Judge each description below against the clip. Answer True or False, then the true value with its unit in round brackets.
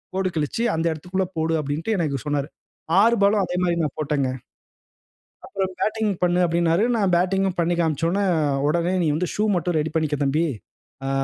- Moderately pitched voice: True (170 Hz)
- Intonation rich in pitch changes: False (3.5 semitones)